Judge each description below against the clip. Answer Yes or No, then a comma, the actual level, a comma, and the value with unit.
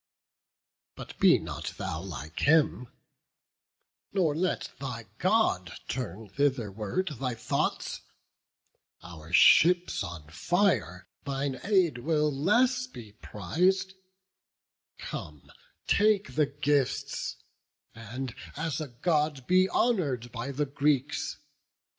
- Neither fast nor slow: No, slow, 100 wpm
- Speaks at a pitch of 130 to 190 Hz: Yes, medium, 140 Hz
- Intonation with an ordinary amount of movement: No, wide, 7.6 semitones